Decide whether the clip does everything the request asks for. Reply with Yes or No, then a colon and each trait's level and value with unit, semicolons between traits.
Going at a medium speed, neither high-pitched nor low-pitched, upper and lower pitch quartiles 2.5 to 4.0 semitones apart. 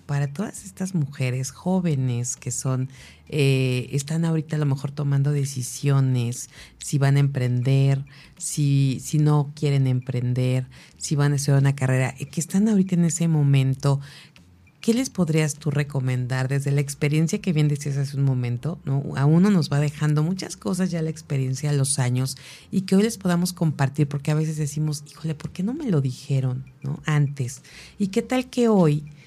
Yes: average, 180 wpm; medium, 145 Hz; average, 2.9 semitones